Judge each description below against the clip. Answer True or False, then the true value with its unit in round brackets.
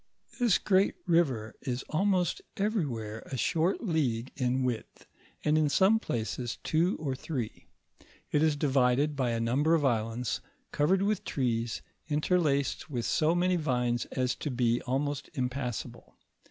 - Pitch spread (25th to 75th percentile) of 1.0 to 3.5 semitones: False (4.9 semitones)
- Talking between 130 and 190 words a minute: True (140 wpm)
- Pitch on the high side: False (140 Hz)